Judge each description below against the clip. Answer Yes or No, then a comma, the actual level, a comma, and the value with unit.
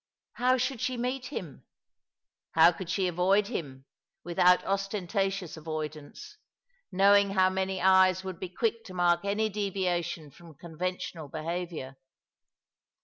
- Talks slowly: Yes, slow, 130 wpm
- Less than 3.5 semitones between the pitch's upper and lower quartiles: Yes, average, 2.8 semitones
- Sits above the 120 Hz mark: Yes, medium, 185 Hz